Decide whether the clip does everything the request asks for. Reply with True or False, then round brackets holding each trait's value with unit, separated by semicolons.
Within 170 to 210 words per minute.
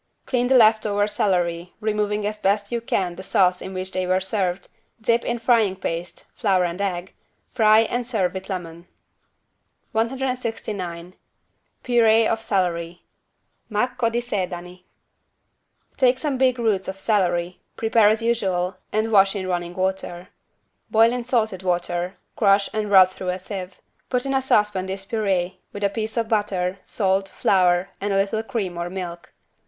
False (160 wpm)